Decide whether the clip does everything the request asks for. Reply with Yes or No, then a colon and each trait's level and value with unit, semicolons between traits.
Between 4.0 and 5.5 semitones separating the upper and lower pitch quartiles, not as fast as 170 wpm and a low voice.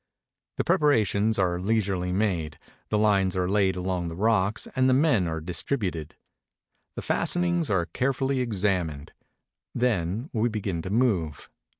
Yes: average, 4.5 semitones; average, 140 wpm; low, 100 Hz